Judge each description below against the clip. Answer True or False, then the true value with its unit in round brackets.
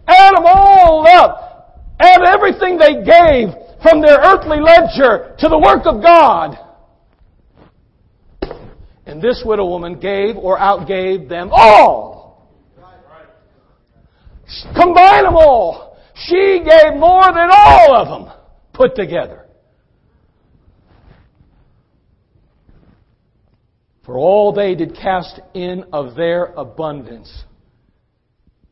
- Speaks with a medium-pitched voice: False (270 Hz)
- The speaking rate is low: True (100 wpm)